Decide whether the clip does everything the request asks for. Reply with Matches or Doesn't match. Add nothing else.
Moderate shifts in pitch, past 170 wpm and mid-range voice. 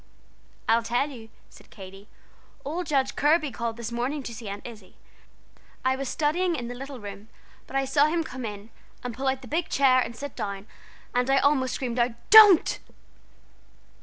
Doesn't match